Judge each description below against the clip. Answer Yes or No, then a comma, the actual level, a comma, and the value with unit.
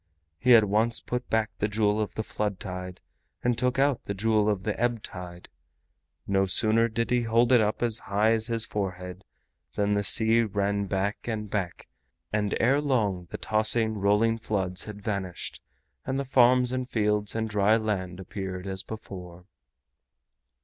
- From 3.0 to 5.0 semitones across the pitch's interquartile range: No, narrow, 2.6 semitones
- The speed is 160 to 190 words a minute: Yes, average, 170 wpm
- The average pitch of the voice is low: Yes, low, 105 Hz